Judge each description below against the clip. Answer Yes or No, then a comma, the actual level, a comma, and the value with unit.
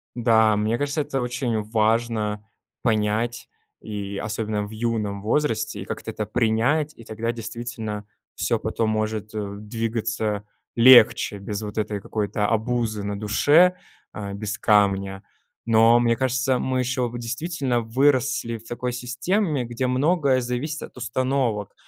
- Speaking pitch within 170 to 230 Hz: No, low, 115 Hz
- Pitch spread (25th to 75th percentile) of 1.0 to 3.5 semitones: Yes, average, 2.9 semitones